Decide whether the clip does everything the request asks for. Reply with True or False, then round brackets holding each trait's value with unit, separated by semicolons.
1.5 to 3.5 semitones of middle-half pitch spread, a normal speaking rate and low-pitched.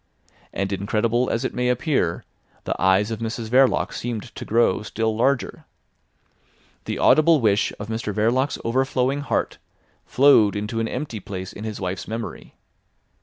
True (3.2 semitones; 150 wpm; 115 Hz)